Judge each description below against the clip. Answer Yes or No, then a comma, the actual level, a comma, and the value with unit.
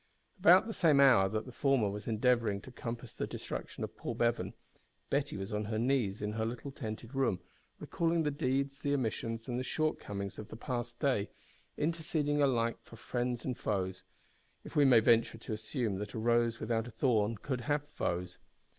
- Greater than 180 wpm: Yes, average, 190 wpm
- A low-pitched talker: Yes, low, 120 Hz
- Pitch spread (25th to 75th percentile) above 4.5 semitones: No, average, 4.0 semitones